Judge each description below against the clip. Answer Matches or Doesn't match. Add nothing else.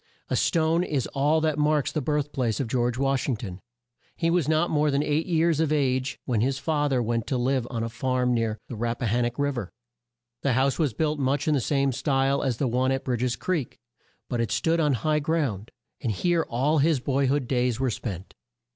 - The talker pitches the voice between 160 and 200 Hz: Doesn't match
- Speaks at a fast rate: Matches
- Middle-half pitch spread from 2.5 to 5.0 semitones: Matches